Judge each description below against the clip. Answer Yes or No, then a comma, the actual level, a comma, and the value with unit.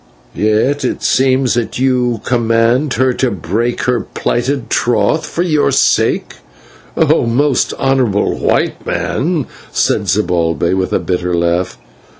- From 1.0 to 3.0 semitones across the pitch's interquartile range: No, average, 4.5 semitones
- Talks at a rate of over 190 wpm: No, slow, 135 wpm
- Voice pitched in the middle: No, low, 120 Hz